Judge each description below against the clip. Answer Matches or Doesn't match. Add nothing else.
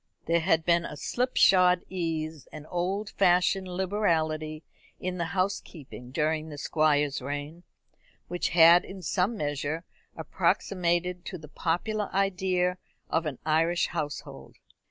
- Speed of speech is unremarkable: Doesn't match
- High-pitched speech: Doesn't match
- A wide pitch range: Doesn't match